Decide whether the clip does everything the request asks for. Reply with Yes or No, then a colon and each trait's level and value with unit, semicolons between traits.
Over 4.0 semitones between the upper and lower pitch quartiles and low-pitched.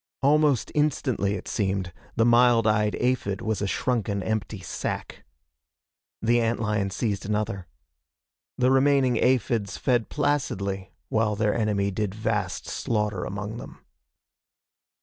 No: average, 3.3 semitones; low, 110 Hz